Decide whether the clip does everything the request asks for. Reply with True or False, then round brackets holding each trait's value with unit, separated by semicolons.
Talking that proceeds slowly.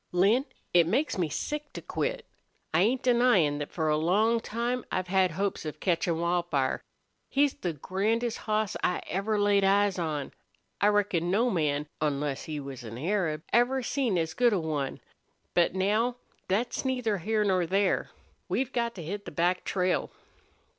False (170 wpm)